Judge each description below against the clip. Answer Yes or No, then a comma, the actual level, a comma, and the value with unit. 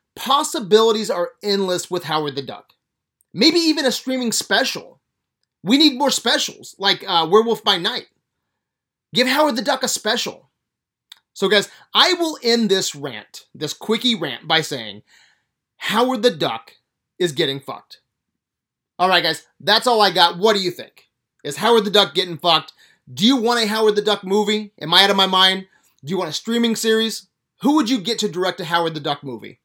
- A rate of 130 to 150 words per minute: No, average, 190 wpm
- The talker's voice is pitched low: No, high, 200 Hz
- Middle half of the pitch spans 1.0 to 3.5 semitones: No, wide, 5.5 semitones